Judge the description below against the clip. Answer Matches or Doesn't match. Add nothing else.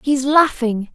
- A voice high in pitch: Matches